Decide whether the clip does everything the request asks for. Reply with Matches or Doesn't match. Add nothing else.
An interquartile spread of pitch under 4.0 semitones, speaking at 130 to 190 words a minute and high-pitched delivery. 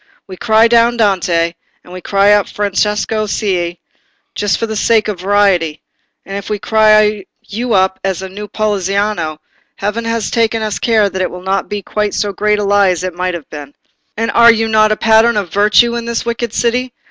Doesn't match